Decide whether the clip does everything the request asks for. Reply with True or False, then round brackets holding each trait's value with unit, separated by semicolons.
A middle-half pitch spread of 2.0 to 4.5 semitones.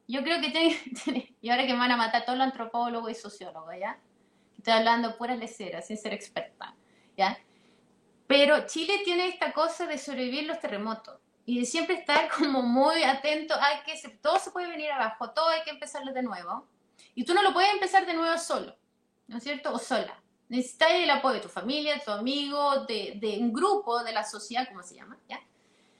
False (5.1 semitones)